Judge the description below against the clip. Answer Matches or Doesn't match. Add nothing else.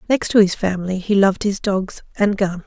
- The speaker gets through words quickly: Matches